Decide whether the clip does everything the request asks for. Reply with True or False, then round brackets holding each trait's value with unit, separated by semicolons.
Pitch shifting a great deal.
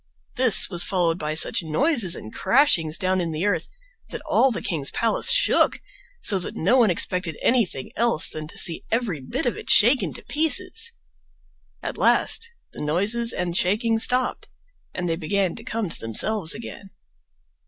True (6.3 semitones)